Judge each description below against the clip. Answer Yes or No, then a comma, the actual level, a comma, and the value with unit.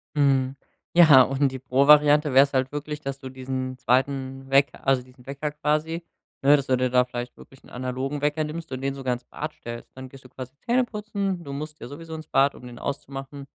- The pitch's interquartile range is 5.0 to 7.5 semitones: No, narrow, 2.4 semitones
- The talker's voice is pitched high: No, low, 135 Hz